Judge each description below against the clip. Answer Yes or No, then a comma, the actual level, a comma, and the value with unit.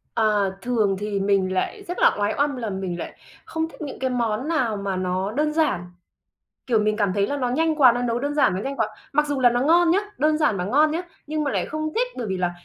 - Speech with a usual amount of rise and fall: No, wide, 6.8 semitones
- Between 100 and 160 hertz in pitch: No, high, 245 Hz